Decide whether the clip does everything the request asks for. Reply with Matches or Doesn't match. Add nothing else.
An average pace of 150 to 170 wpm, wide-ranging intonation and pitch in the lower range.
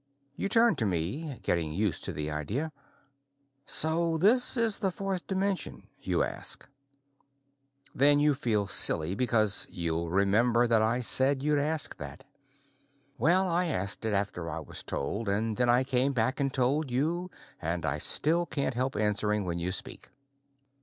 Matches